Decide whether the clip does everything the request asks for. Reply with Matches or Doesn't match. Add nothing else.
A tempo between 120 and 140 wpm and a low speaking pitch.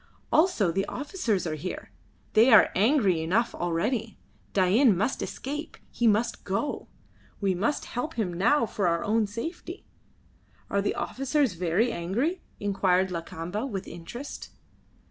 Doesn't match